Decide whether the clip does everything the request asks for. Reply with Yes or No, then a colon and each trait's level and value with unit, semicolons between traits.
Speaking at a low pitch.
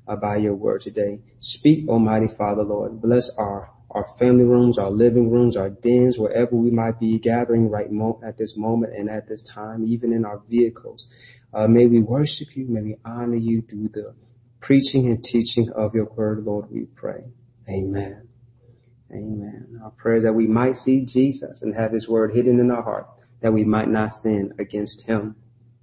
Yes: low, 115 Hz